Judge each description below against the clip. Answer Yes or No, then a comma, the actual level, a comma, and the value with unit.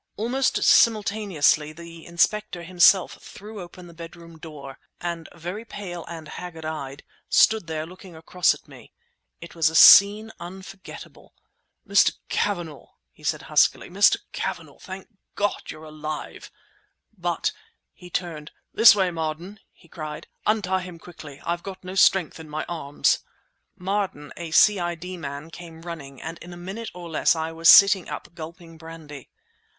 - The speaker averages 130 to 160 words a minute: Yes, average, 140 wpm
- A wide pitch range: No, average, 2.9 semitones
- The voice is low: No, medium, 170 Hz